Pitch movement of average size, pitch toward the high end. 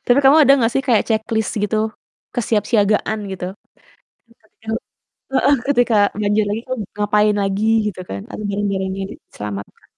No: narrow, 2.2 semitones; high, 215 Hz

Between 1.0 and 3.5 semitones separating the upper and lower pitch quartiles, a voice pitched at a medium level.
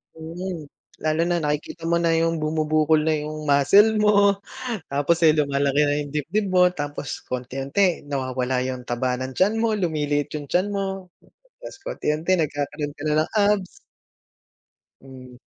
No: average, 4.1 semitones; medium, 155 Hz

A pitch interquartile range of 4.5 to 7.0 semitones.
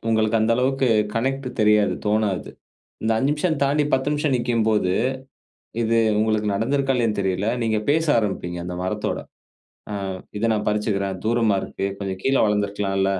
No: average, 3.9 semitones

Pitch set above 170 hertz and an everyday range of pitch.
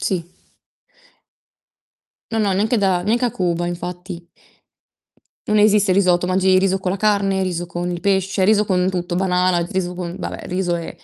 No: medium, 185 Hz; narrow, 1.9 semitones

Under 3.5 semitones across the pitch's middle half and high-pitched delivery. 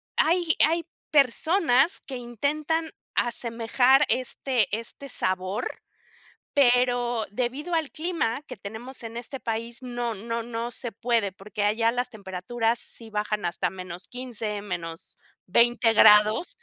Yes: average, 3.1 semitones; high, 240 Hz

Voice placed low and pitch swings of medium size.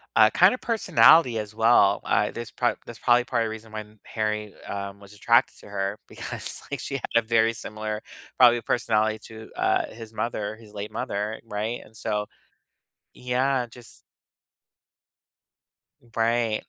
No: low, 110 Hz; narrow, 1.9 semitones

